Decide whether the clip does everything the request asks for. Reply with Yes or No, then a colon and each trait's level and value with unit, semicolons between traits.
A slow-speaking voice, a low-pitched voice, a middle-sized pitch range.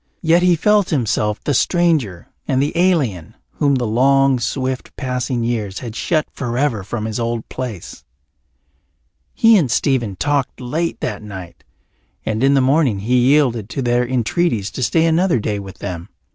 No: average, 160 wpm; low, 125 Hz; average, 5.0 semitones